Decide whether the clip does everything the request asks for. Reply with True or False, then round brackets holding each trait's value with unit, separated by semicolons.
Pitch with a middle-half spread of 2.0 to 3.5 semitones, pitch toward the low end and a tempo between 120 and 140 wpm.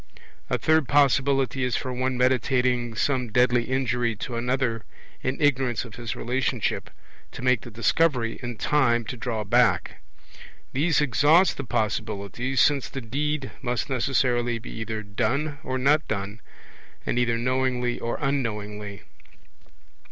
True (2.6 semitones; 125 Hz; 135 wpm)